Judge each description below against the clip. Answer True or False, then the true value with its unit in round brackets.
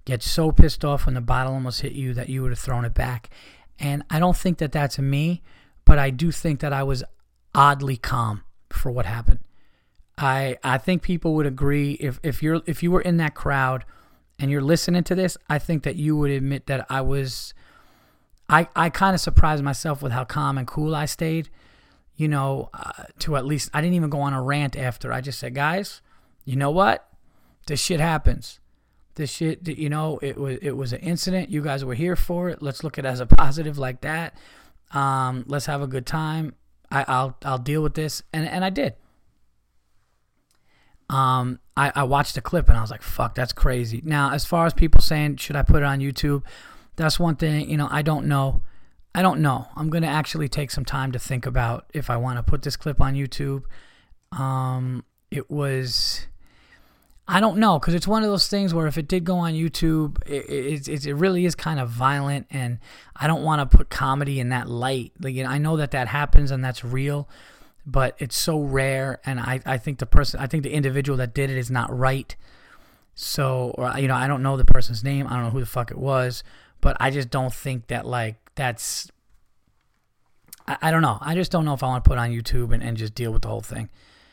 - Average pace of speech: False (225 wpm)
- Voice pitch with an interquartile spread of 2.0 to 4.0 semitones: True (3.2 semitones)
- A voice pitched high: False (140 Hz)